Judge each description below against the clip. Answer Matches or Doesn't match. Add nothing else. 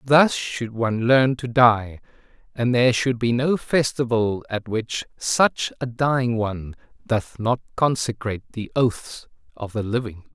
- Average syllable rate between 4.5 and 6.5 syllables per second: Doesn't match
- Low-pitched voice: Matches